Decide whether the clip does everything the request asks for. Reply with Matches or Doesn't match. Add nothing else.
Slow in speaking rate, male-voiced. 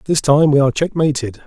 Doesn't match